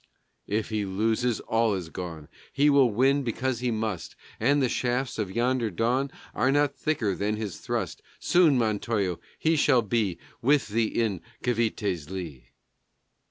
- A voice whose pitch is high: No, low, 115 Hz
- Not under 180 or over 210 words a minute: No, average, 155 wpm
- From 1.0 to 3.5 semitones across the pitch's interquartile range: No, average, 4.3 semitones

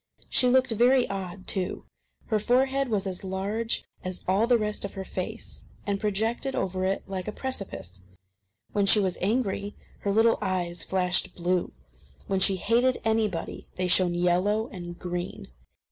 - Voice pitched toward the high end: Yes, high, 195 Hz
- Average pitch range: Yes, average, 3.4 semitones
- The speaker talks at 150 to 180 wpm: Yes, average, 160 wpm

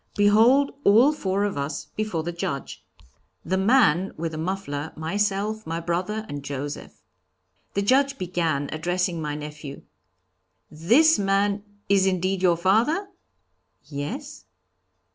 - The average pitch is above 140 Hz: Yes, high, 190 Hz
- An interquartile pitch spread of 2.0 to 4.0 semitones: No, average, 4.9 semitones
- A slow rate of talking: Yes, slow, 125 wpm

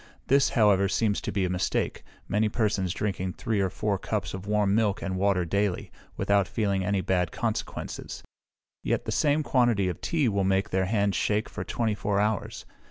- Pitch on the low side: Yes, low, 100 Hz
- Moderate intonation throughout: No, narrow, 2.1 semitones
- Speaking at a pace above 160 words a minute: Yes, average, 185 wpm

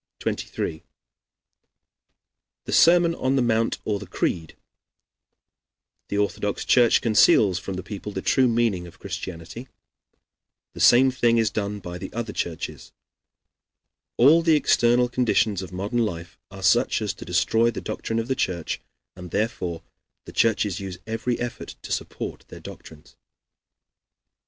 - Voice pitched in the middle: No, low, 105 Hz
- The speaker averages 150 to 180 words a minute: No, average, 140 wpm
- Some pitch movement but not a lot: Yes, average, 4.2 semitones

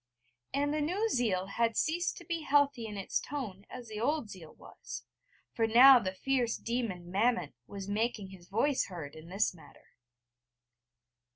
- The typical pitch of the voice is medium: No, high, 230 Hz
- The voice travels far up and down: Yes, wide, 6.1 semitones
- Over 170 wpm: No, average, 165 wpm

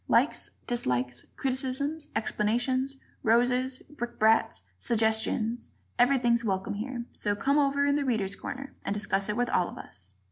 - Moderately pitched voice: No, high, 235 Hz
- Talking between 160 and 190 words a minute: No, average, 140 wpm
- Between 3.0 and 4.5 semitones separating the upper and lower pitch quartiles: Yes, average, 4.0 semitones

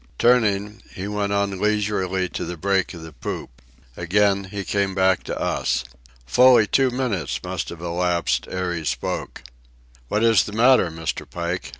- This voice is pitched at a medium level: No, low, 100 Hz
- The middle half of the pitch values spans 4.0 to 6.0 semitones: No, average, 3.1 semitones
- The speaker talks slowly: No, average, 165 wpm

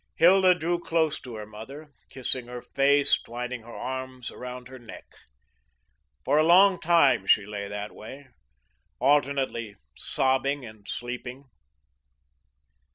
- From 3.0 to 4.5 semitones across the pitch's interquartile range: Yes, average, 3.5 semitones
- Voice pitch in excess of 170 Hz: No, low, 130 Hz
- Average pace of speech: No, slow, 125 wpm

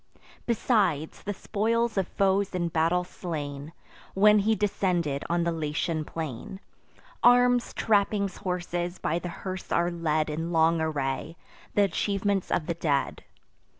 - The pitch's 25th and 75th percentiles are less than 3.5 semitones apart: No, average, 3.9 semitones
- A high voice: No, medium, 175 Hz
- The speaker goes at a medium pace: No, slow, 130 wpm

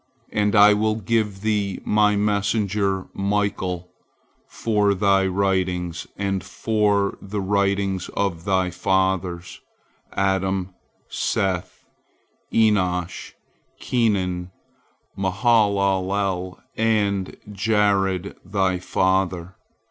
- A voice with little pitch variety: Yes, narrow, 1.7 semitones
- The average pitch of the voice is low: Yes, low, 100 Hz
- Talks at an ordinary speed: No, slow, 80 wpm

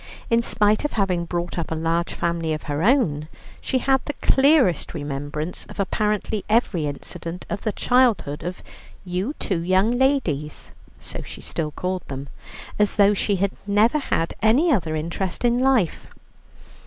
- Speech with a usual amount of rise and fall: No, wide, 6.0 semitones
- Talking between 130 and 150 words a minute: No, average, 160 wpm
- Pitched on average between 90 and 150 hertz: No, high, 190 Hz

